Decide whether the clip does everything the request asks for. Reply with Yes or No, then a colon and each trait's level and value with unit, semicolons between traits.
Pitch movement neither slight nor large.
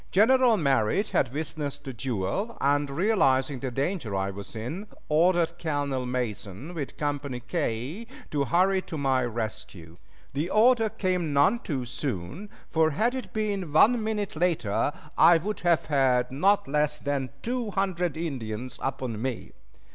No: wide, 6.4 semitones